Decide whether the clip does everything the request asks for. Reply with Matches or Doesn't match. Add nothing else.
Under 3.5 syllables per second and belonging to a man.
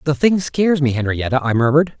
Doesn't match